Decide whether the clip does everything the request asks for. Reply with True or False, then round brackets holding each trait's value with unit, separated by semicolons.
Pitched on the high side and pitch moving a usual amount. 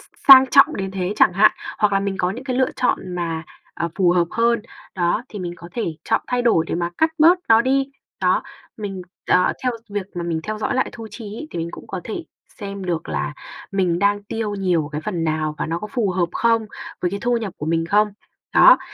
True (200 Hz; 4.9 semitones)